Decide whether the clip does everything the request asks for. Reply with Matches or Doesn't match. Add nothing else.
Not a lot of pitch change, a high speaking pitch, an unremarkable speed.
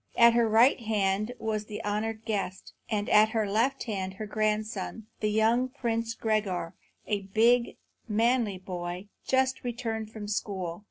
Matches